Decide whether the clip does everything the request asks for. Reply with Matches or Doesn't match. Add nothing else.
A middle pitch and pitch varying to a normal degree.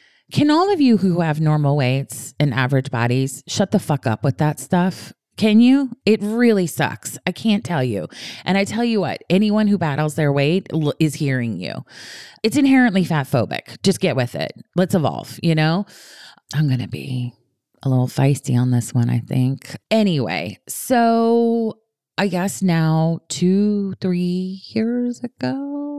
Doesn't match